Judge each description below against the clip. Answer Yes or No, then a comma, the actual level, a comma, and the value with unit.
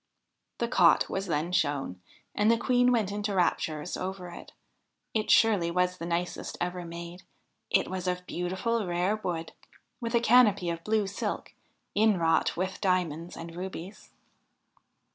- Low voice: No, medium, 180 Hz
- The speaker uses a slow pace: No, average, 145 wpm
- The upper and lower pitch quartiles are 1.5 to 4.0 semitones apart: Yes, average, 3.5 semitones